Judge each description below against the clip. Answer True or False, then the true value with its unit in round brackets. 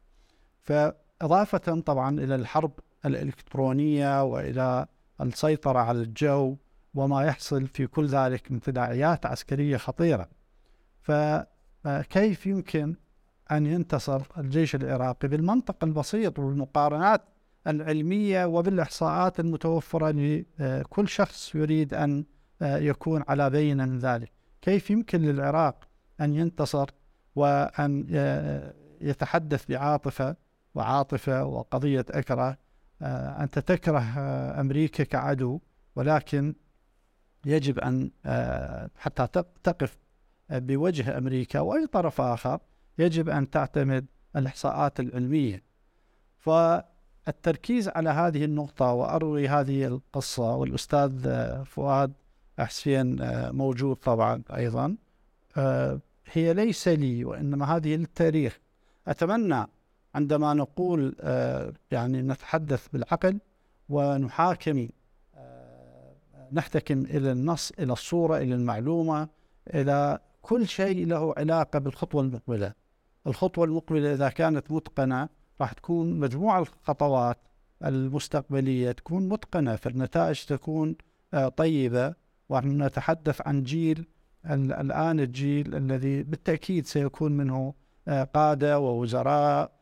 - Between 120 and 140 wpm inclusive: False (95 wpm)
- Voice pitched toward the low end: False (145 Hz)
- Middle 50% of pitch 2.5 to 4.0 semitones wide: True (3.4 semitones)